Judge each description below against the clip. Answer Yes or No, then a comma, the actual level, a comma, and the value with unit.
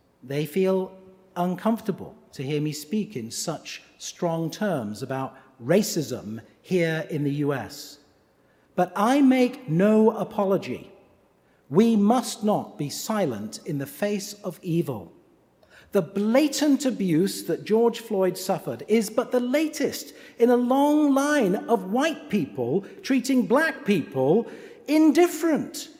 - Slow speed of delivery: Yes, slow, 125 wpm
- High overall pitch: Yes, high, 200 Hz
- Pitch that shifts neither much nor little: No, wide, 7.8 semitones